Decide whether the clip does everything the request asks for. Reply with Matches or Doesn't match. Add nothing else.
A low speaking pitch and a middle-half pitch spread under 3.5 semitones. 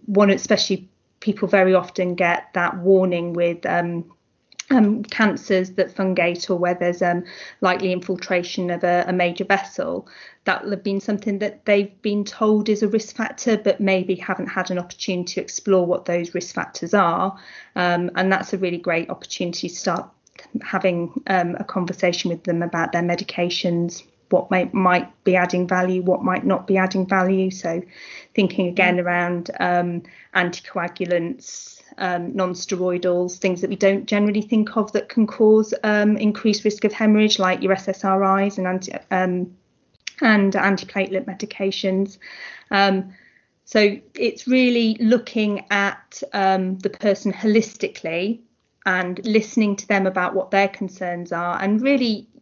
Doesn't match